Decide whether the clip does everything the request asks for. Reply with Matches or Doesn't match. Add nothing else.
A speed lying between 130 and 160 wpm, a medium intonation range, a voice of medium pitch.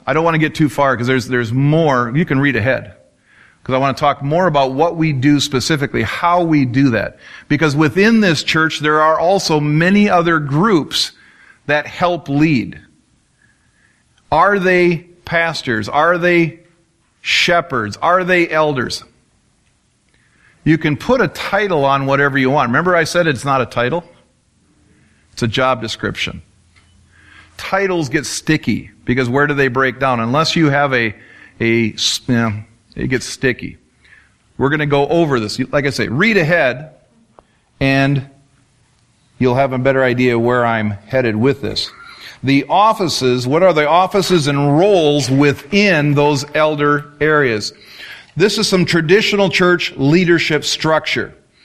Matches